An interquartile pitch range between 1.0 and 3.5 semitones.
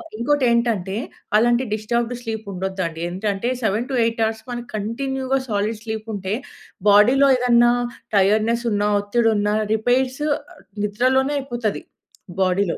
Yes: average, 2.9 semitones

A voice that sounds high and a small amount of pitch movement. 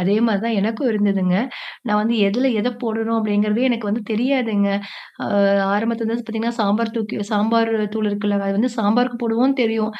Yes: high, 225 Hz; narrow, 1.9 semitones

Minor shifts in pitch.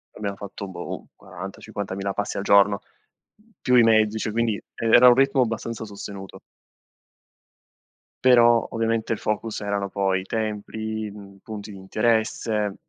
Yes: narrow, 2.2 semitones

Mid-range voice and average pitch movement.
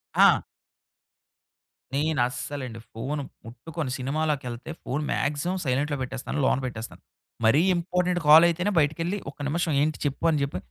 Yes: medium, 145 Hz; average, 4.0 semitones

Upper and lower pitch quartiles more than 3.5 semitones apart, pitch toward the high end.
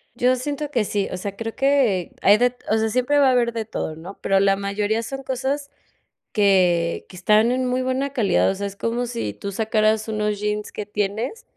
Yes: average, 4.1 semitones; high, 220 Hz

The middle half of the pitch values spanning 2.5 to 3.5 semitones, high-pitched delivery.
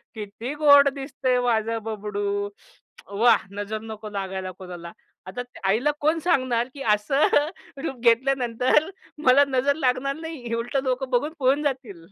No: average, 4.4 semitones; high, 245 Hz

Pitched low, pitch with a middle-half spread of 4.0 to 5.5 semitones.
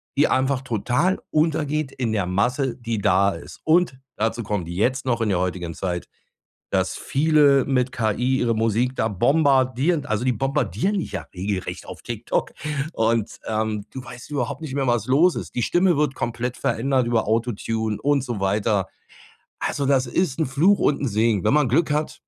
Yes: low, 125 Hz; average, 4.3 semitones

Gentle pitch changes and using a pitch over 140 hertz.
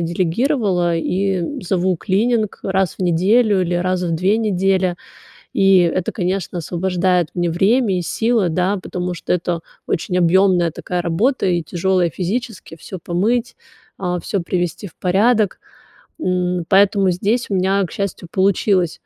Yes: narrow, 2.2 semitones; medium, 185 Hz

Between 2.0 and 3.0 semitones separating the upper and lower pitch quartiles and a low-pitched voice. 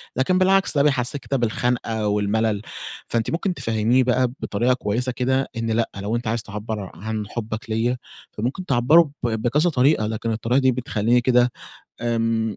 Yes: narrow, 2.6 semitones; low, 120 Hz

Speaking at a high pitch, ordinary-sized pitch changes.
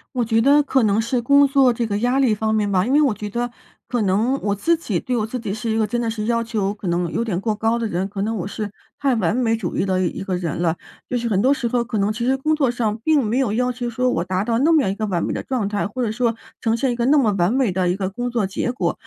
Yes: high, 225 Hz; average, 3.6 semitones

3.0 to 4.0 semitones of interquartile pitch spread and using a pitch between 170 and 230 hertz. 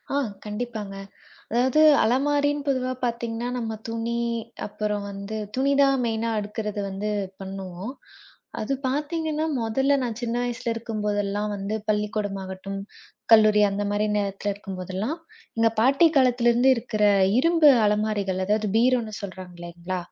Yes: average, 3.6 semitones; high, 220 Hz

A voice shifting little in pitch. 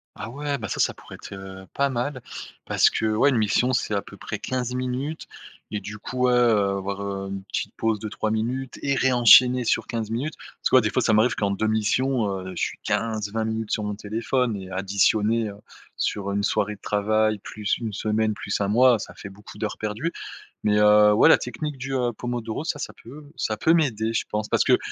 No: average, 3.3 semitones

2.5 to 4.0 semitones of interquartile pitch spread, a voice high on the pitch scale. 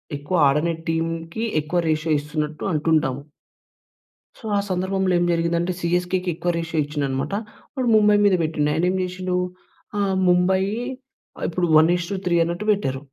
No: average, 2.8 semitones; medium, 170 Hz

